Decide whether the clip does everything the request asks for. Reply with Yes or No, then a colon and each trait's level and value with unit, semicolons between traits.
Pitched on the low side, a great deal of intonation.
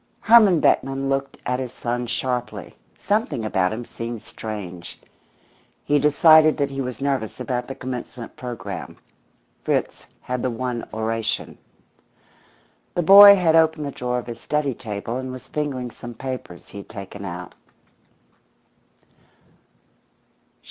No: low, 125 Hz; average, 3.9 semitones